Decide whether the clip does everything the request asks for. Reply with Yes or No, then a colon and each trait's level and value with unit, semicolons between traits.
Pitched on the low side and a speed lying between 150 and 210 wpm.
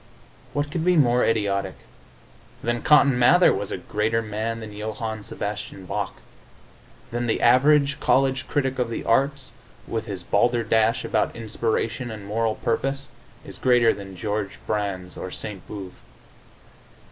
No: low, 115 Hz; average, 140 wpm